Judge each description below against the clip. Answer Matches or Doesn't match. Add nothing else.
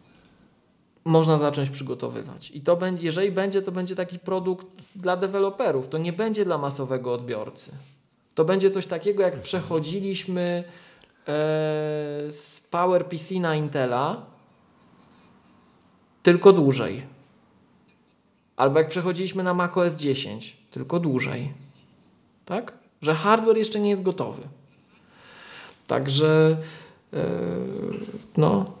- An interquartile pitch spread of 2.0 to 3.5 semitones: Doesn't match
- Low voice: Doesn't match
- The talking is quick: Doesn't match